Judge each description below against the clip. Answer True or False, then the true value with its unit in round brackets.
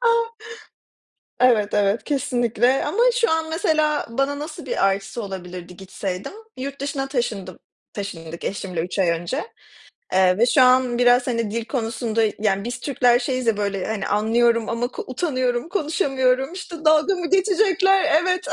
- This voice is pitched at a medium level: False (245 Hz)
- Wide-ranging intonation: True (6.2 semitones)